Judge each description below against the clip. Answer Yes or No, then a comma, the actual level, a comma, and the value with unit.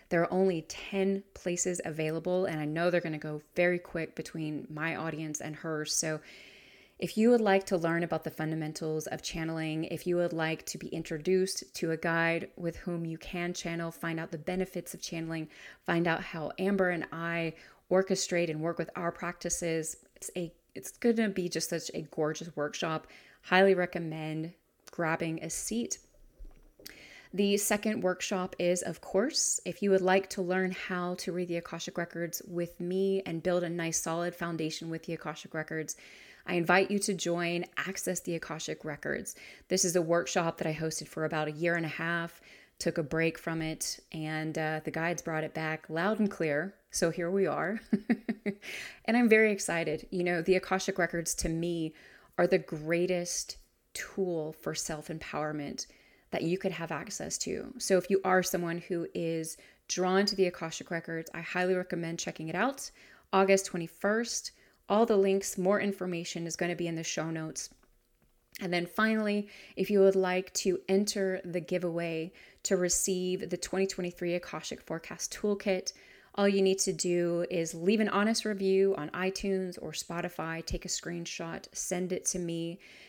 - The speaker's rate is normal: Yes, average, 180 wpm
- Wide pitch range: No, narrow, 2.4 semitones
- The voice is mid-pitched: Yes, medium, 175 Hz